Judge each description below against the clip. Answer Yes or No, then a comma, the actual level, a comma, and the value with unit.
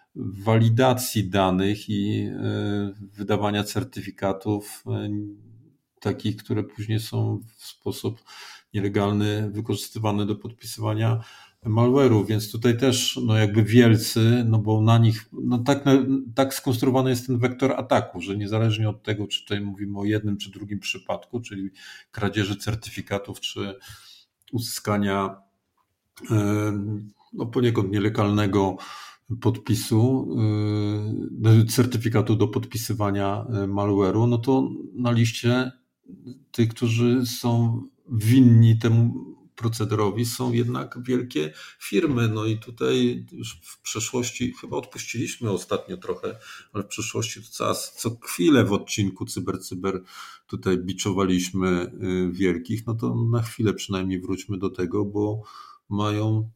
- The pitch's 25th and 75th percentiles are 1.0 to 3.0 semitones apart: Yes, average, 2.7 semitones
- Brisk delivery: No, average, 120 wpm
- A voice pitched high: No, low, 110 Hz